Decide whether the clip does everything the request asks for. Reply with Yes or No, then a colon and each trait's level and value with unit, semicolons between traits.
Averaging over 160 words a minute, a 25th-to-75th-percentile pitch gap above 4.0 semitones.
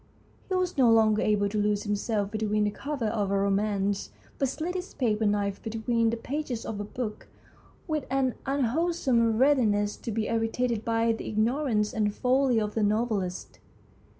No: average, 175 wpm; average, 3.5 semitones